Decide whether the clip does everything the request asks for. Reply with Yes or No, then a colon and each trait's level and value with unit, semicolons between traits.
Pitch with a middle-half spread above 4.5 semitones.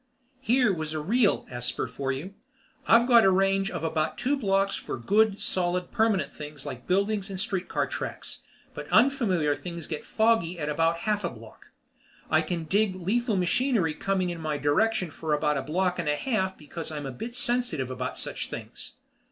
Yes: wide, 5.6 semitones